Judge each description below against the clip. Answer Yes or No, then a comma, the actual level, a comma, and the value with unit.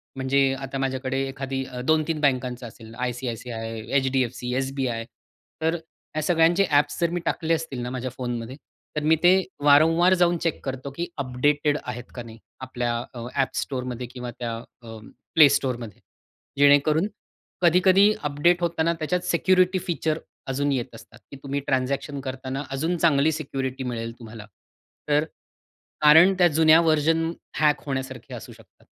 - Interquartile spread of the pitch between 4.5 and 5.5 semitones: No, average, 4.1 semitones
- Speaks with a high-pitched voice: No, medium, 140 Hz